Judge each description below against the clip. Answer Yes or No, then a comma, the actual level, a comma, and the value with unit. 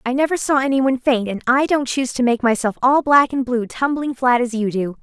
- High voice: Yes, very high, 255 Hz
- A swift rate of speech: Yes, fast, 250 wpm